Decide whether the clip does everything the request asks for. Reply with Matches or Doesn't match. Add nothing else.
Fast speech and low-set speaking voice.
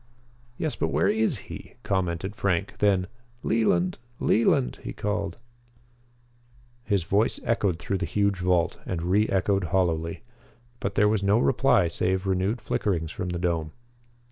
Doesn't match